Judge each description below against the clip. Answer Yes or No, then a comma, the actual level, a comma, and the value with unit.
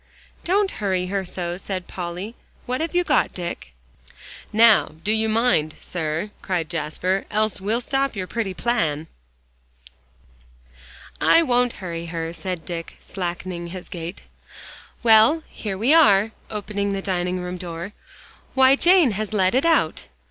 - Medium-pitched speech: No, high, 195 Hz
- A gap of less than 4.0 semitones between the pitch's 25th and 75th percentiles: No, average, 4.6 semitones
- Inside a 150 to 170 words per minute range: No, average, 140 wpm